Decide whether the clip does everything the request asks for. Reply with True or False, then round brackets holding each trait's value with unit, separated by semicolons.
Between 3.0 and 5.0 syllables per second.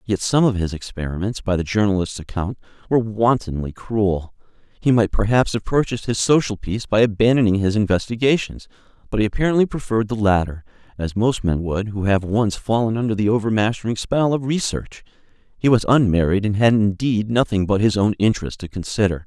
False (5.8 syllables/s)